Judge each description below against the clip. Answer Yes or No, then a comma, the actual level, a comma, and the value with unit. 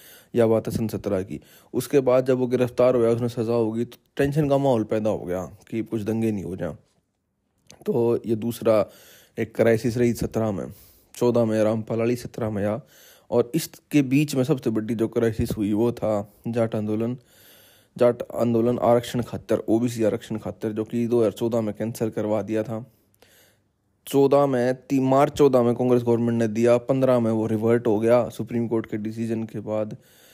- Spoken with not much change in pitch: Yes, narrow, 1.9 semitones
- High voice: No, low, 115 Hz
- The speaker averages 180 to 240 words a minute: Yes, fast, 190 wpm